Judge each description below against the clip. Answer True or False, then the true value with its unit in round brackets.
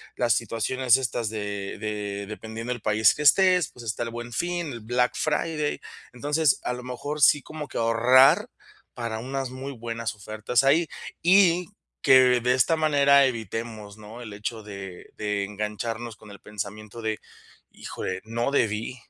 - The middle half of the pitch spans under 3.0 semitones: False (3.9 semitones)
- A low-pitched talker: True (120 Hz)